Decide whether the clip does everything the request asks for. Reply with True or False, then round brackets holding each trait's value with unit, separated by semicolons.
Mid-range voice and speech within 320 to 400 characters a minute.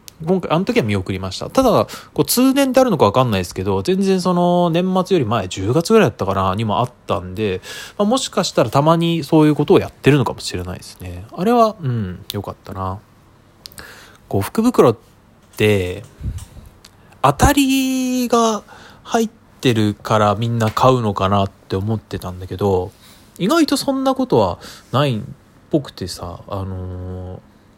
False (115 Hz; 330 characters per minute)